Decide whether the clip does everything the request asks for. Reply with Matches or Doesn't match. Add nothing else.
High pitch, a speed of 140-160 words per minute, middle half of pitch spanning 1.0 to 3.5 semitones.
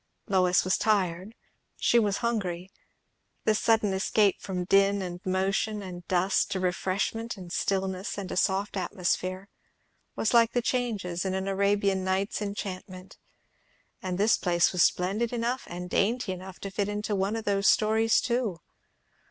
Matches